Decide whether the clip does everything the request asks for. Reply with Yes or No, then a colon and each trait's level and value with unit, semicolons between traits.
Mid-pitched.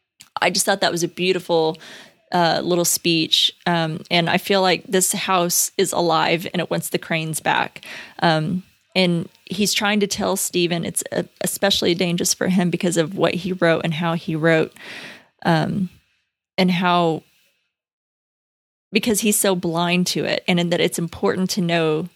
Yes: medium, 175 Hz